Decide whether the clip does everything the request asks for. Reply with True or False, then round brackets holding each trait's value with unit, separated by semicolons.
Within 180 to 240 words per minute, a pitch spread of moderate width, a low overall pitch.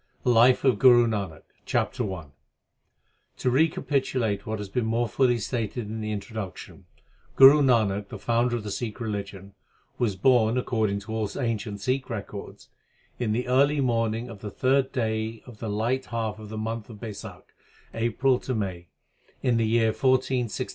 False (160 wpm; 3.0 semitones; 115 Hz)